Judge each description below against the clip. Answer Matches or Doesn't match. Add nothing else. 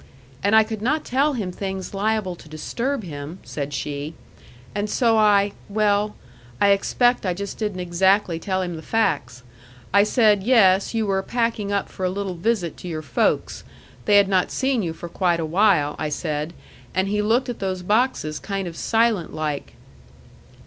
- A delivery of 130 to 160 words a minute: Doesn't match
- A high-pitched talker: Matches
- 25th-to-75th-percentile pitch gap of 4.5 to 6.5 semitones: Doesn't match